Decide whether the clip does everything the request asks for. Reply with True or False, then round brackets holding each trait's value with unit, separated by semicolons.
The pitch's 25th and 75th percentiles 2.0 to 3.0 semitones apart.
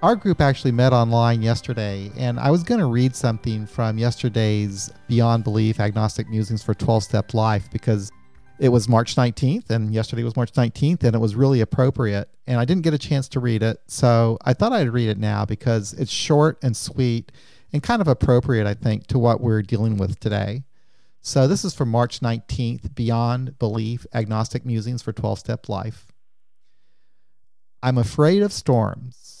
True (2.7 semitones)